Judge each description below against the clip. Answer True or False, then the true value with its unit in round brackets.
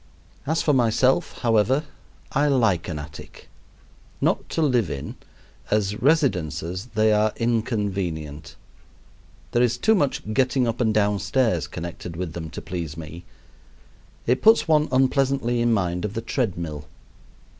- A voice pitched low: True (110 Hz)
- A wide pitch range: True (6.7 semitones)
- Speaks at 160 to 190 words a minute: False (145 wpm)